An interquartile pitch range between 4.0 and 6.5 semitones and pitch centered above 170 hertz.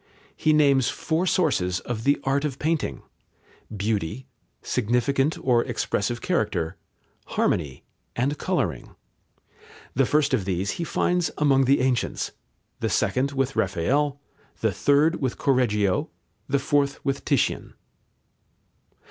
No: average, 4.9 semitones; low, 135 Hz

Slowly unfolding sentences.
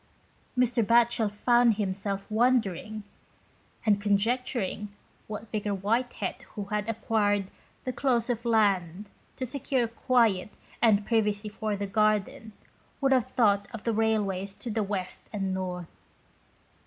Yes: slow, 130 wpm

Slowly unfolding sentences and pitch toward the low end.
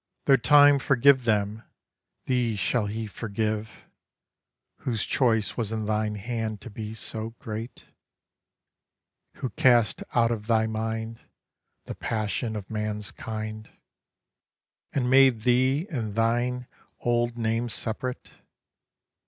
Yes: slow, 115 wpm; low, 115 Hz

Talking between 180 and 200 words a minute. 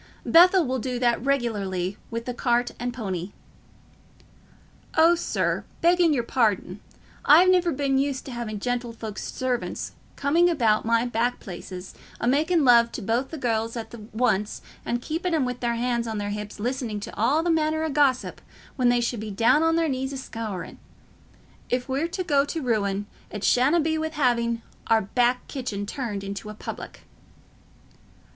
No: average, 170 wpm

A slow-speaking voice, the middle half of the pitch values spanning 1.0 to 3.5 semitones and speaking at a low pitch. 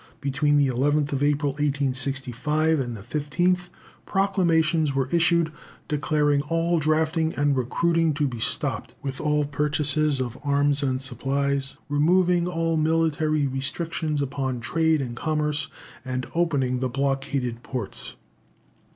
No: slow, 125 wpm; average, 2.8 semitones; medium, 145 Hz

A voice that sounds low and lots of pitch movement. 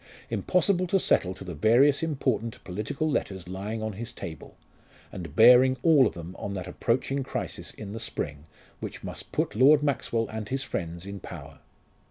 Yes: low, 110 Hz; wide, 6.1 semitones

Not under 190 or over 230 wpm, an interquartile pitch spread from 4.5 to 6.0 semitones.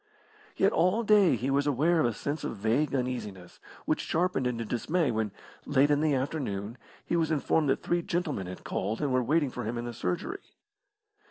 Yes: average, 195 wpm; wide, 5.5 semitones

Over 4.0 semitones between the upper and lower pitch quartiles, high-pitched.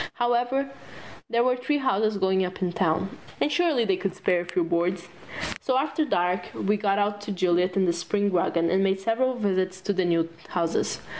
Yes: average, 4.9 semitones; high, 195 Hz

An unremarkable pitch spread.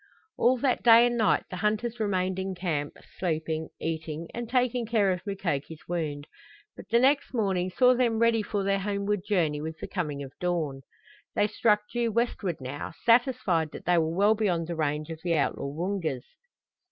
No: wide, 5.8 semitones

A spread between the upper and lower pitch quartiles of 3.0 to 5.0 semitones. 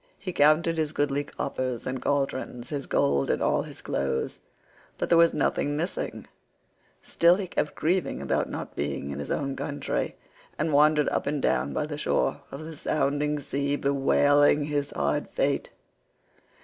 No: narrow, 2.5 semitones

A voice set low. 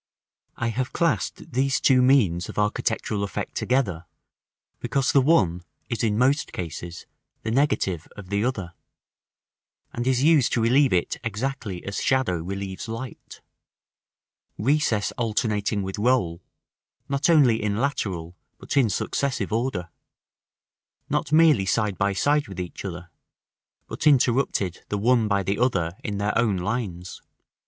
Yes: low, 110 Hz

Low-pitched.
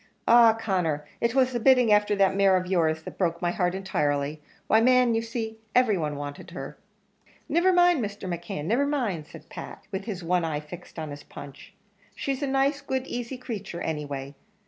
No: high, 195 Hz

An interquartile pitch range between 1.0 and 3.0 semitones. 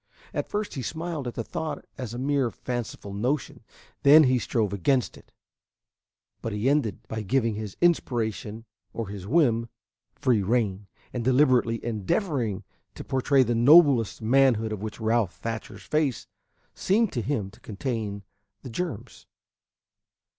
No: average, 4.1 semitones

